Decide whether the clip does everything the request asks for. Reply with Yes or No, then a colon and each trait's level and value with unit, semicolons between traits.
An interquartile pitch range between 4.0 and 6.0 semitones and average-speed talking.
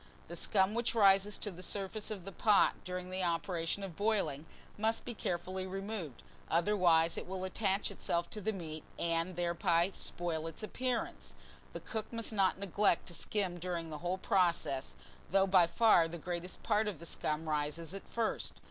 No: average, 3.4 semitones; average, 175 wpm